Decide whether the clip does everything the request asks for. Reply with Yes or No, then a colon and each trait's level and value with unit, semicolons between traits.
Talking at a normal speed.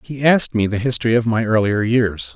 No: fast, 230 wpm